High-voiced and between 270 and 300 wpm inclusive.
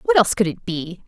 Yes: high, 200 Hz; fast, 280 wpm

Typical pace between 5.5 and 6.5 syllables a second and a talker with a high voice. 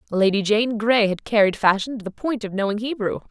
Yes: 5.6 syllables/s; high, 215 Hz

